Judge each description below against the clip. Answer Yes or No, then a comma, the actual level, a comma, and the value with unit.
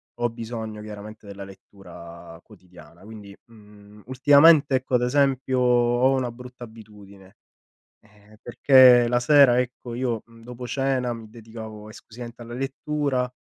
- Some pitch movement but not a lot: Yes, average, 3.0 semitones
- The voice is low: Yes, low, 120 Hz